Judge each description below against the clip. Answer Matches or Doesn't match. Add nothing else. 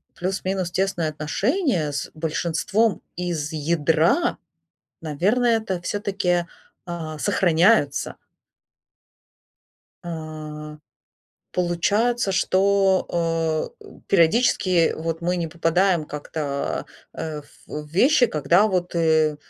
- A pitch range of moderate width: Matches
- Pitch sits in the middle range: Matches